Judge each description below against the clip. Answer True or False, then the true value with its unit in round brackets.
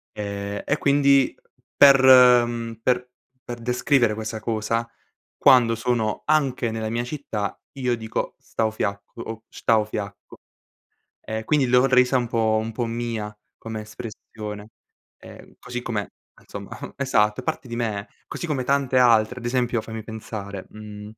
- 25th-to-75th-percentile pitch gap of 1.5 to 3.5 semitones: True (2.6 semitones)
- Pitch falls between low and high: False (115 Hz)